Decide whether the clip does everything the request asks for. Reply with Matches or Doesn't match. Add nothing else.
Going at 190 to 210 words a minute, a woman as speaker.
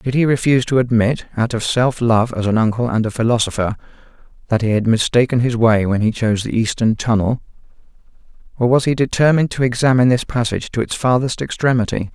Doesn't match